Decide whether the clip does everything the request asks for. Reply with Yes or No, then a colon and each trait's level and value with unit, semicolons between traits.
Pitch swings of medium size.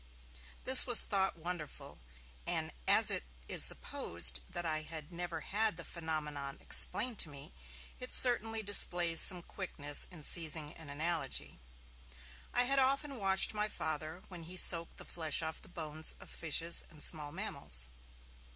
Yes: average, 3.9 semitones